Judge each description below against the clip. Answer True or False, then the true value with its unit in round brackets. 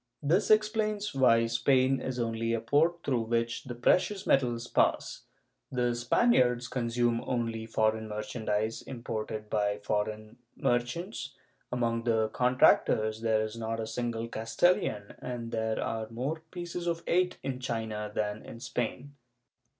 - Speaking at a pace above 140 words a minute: False (135 wpm)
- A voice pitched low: True (120 Hz)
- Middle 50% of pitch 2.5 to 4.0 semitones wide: True (2.9 semitones)